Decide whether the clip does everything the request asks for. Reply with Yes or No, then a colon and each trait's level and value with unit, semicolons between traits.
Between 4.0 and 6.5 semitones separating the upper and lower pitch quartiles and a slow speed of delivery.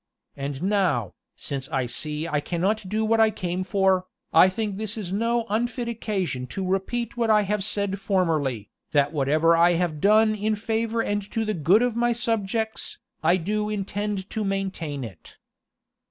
No: average, 4.7 semitones; average, 170 wpm